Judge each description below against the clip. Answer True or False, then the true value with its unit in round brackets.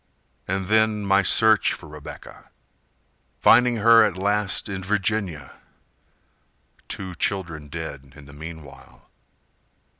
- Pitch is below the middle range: True (95 Hz)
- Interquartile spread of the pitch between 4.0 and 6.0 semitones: True (4.8 semitones)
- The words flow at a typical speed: False (110 wpm)